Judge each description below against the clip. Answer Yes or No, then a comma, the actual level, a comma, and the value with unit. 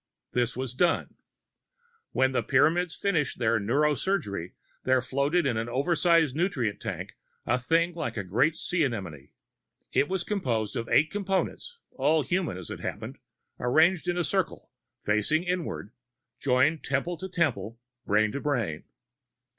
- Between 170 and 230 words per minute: No, average, 145 wpm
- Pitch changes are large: Yes, wide, 6.6 semitones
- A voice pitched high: No, medium, 140 Hz